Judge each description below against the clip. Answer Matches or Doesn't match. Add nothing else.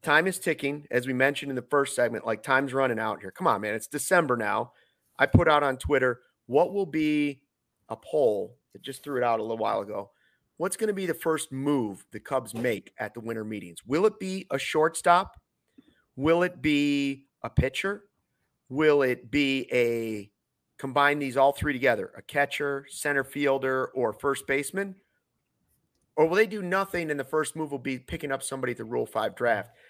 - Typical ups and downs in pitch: Matches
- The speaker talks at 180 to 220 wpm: Matches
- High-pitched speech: Doesn't match